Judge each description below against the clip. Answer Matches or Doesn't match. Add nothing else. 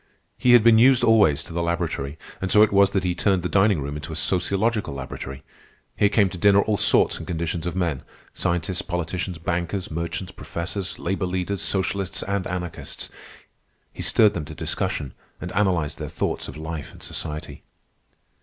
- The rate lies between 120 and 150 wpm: Doesn't match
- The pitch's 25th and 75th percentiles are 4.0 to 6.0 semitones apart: Doesn't match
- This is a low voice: Matches